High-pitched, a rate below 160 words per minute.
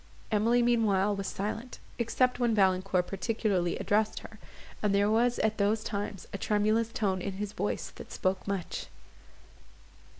Yes: high, 210 Hz; average, 145 wpm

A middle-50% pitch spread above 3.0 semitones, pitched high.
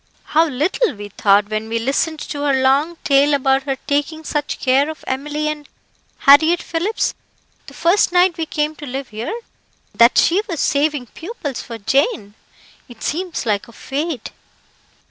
Yes: average, 3.7 semitones; very high, 290 Hz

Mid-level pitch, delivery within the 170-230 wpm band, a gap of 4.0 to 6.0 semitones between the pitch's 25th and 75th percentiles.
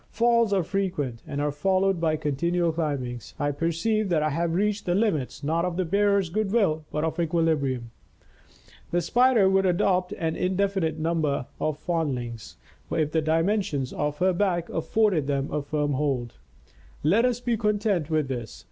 Yes: medium, 165 Hz; average, 175 wpm; average, 4.7 semitones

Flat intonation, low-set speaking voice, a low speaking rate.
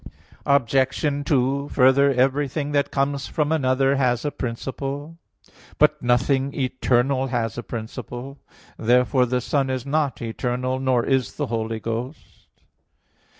Yes: narrow, 2.3 semitones; low, 130 Hz; slow, 125 wpm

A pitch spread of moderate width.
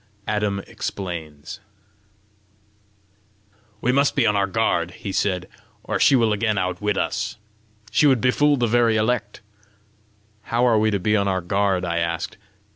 Yes: average, 3.8 semitones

